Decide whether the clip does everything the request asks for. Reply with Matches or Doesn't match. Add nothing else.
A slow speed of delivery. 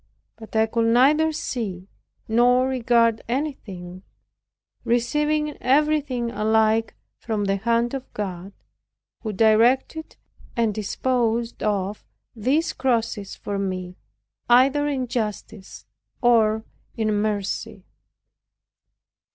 Matches